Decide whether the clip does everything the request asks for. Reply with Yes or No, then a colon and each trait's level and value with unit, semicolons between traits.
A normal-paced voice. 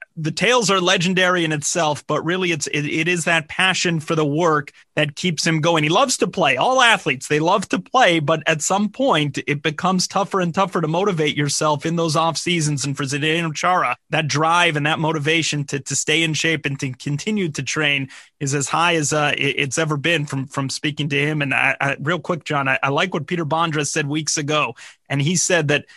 No: fast, 225 wpm